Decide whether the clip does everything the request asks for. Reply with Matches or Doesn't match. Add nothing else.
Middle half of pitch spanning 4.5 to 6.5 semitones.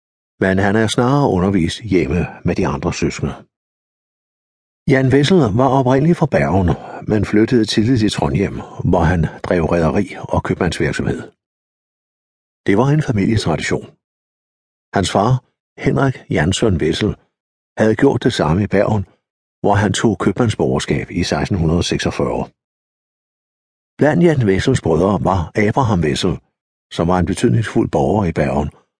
Matches